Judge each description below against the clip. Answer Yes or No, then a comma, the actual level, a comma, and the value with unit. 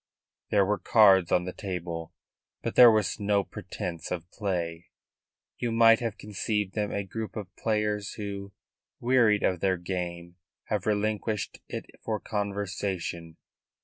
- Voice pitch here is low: Yes, low, 100 Hz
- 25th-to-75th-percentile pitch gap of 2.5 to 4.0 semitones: Yes, average, 2.9 semitones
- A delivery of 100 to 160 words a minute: Yes, average, 140 wpm